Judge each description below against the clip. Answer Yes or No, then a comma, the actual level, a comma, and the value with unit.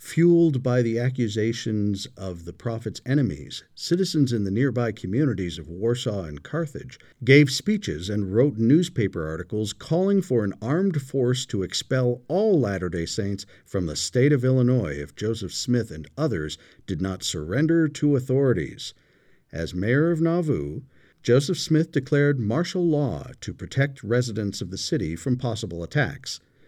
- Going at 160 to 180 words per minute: No, average, 150 wpm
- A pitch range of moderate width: No, wide, 6.7 semitones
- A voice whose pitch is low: Yes, low, 120 Hz